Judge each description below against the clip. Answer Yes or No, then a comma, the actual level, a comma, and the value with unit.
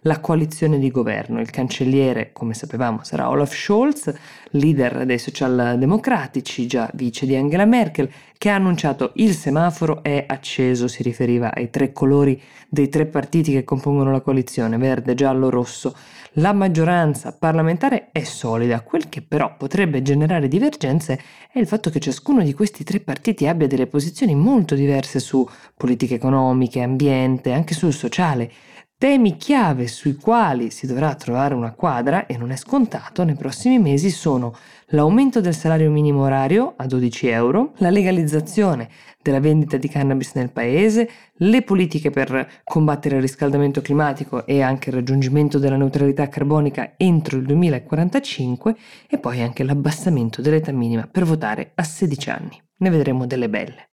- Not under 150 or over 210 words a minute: Yes, average, 155 wpm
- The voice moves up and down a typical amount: Yes, average, 4.3 semitones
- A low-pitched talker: No, medium, 145 Hz